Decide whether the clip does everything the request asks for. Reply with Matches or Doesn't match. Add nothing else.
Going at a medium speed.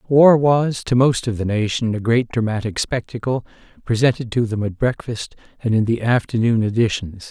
Matches